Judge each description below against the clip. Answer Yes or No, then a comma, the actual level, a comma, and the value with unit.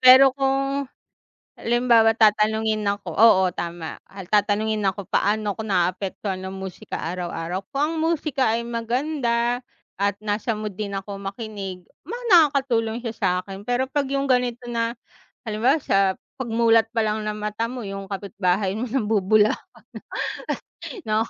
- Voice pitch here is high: Yes, high, 220 Hz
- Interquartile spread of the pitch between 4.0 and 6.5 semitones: No, average, 3.6 semitones